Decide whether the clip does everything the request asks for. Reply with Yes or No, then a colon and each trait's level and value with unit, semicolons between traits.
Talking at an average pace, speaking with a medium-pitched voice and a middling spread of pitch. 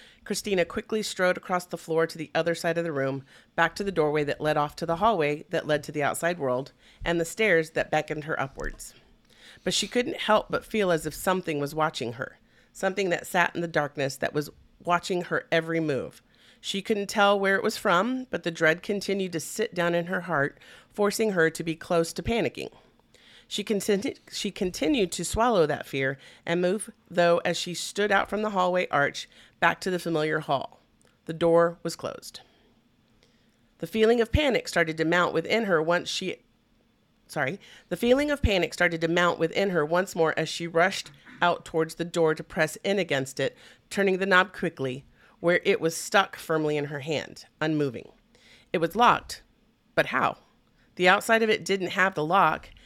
Yes: average, 195 wpm; medium, 170 Hz; average, 3.6 semitones